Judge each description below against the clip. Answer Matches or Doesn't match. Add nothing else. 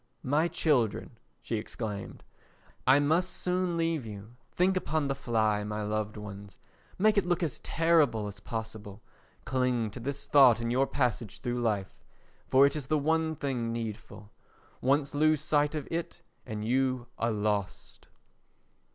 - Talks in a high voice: Doesn't match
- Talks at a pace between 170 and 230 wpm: Doesn't match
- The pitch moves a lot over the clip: Matches